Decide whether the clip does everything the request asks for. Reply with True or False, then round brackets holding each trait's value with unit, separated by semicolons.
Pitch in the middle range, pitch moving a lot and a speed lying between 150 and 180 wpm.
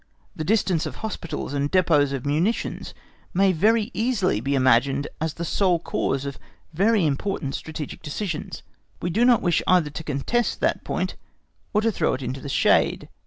True (160 Hz; 6.0 semitones; 170 wpm)